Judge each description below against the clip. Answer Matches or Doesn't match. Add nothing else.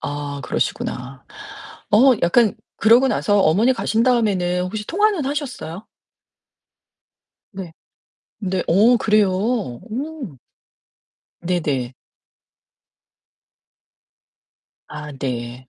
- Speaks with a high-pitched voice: Matches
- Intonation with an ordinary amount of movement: Doesn't match